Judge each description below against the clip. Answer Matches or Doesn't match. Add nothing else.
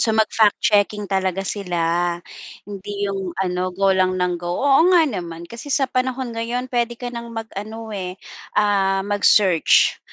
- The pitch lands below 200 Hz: Doesn't match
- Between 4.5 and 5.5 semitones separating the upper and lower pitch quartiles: Doesn't match